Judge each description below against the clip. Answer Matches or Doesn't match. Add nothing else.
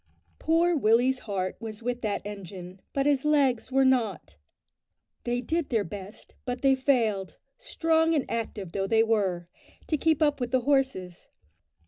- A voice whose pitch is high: Matches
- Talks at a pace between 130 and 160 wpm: Matches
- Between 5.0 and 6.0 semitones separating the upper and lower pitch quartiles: Matches